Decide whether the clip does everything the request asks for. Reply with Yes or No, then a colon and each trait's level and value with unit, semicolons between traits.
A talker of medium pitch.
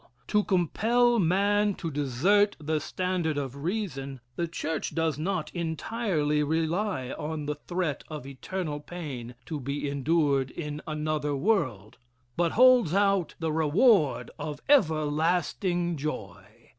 Yes: medium, 160 Hz